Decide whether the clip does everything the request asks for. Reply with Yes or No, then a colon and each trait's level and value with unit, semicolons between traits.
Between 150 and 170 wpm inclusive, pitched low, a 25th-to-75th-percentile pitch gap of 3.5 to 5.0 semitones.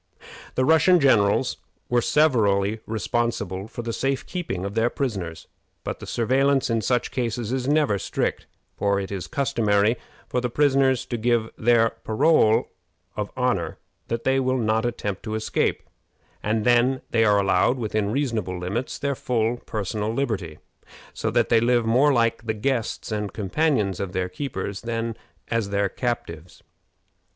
Yes: average, 155 wpm; low, 115 Hz; average, 3.8 semitones